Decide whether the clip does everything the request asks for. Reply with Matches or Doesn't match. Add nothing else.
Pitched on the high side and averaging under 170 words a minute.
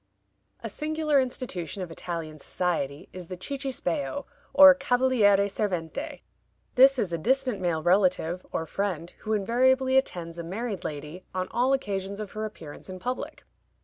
Matches